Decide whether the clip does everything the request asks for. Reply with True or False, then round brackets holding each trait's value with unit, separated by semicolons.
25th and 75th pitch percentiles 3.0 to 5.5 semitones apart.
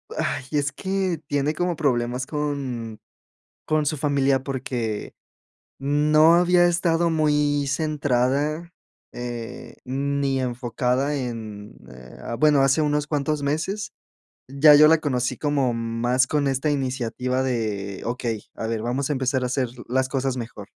True (3.3 semitones)